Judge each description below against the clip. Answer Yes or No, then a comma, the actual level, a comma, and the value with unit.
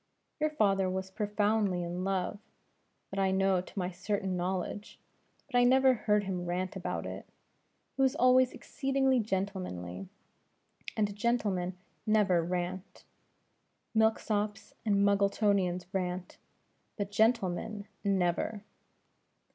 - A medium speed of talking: No, slow, 115 wpm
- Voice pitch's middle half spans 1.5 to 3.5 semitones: Yes, average, 2.9 semitones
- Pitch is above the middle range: Yes, high, 200 Hz